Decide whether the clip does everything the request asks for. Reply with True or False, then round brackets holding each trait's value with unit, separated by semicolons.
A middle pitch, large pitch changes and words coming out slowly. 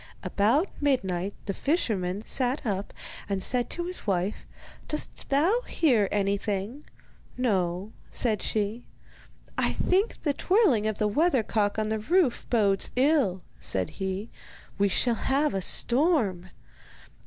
False (220 Hz; 6.2 semitones; 130 wpm)